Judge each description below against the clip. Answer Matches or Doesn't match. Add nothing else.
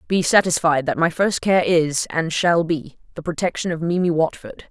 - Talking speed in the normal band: Matches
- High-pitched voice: Doesn't match